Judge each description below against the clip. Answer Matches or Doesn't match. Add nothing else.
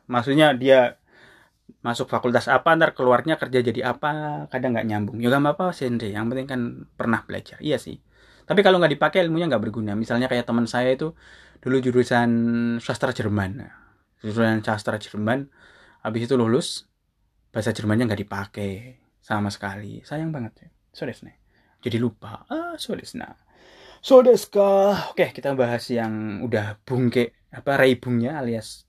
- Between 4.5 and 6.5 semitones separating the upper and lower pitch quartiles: Doesn't match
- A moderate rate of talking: Doesn't match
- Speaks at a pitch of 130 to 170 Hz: Doesn't match